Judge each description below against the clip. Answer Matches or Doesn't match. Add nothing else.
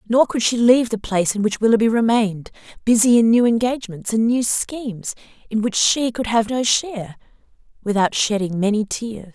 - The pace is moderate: Matches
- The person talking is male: Doesn't match